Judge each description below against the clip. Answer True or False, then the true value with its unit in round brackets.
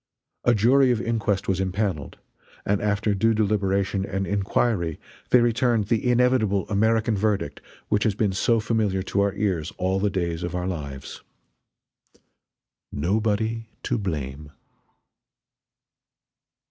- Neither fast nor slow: False (125 wpm)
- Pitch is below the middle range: True (100 Hz)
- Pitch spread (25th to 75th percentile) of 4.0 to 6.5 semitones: False (2.9 semitones)